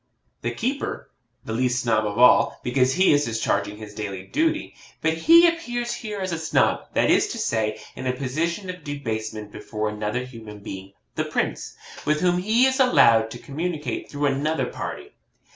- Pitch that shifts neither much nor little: No, wide, 8.5 semitones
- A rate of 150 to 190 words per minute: Yes, average, 180 wpm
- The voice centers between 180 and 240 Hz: No, low, 135 Hz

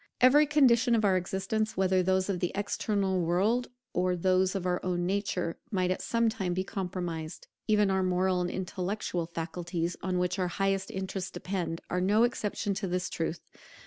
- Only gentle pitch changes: Yes, narrow, 2.1 semitones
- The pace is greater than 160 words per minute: Yes, average, 175 wpm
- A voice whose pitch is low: No, medium, 185 Hz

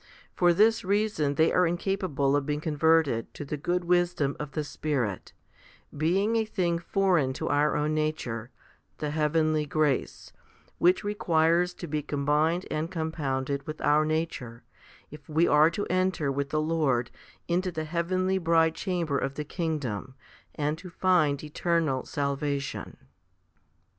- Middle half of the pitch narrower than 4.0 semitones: Yes, average, 3.2 semitones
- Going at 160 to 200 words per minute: No, average, 145 wpm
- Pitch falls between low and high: Yes, medium, 155 Hz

